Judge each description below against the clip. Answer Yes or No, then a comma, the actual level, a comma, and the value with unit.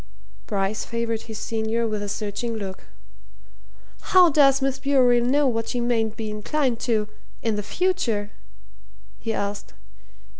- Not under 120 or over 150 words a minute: Yes, average, 140 wpm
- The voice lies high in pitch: Yes, high, 230 Hz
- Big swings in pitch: No, average, 3.4 semitones